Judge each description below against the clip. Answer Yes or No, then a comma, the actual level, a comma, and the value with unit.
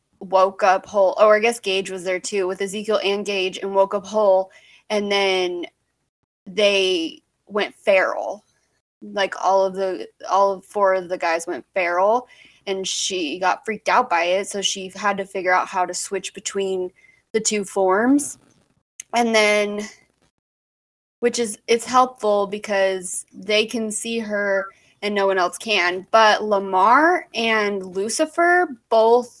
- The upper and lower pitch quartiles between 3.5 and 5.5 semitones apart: No, narrow, 2.6 semitones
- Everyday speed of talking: Yes, average, 155 wpm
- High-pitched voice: Yes, high, 200 Hz